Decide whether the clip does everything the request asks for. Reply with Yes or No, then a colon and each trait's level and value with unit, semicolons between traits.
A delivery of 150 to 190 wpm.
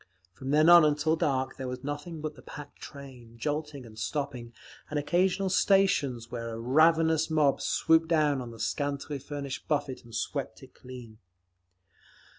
Yes: average, 160 wpm